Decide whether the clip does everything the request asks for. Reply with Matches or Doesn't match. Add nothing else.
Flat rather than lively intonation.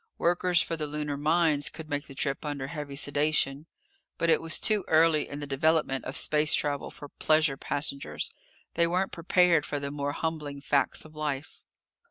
Matches